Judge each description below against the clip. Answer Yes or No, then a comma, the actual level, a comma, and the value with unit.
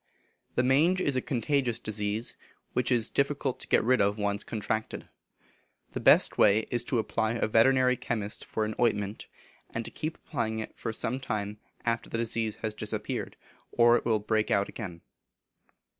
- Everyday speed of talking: Yes, average, 185 wpm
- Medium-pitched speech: No, low, 115 Hz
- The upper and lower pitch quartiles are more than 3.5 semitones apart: No, average, 2.8 semitones